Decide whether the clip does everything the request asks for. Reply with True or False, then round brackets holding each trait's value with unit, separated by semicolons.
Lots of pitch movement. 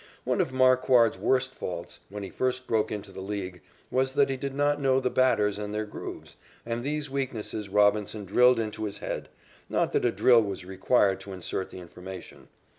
False (4.6 semitones)